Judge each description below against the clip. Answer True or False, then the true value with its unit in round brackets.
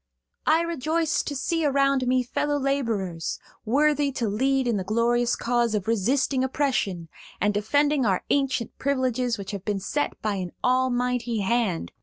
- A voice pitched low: False (250 Hz)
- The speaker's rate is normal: True (155 wpm)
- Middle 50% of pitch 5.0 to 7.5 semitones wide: False (4.5 semitones)